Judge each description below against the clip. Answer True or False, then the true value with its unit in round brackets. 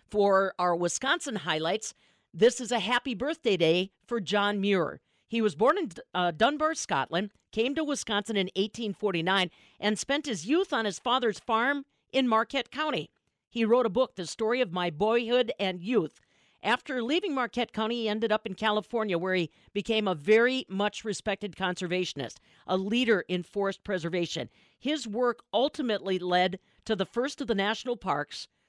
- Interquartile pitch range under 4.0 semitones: False (4.3 semitones)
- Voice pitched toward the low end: False (215 Hz)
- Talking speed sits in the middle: True (165 wpm)